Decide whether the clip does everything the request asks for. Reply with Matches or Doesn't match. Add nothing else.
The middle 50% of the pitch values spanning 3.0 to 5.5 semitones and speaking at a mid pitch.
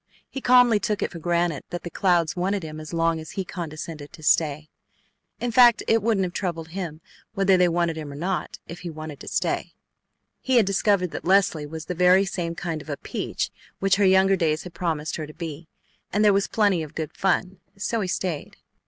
Matches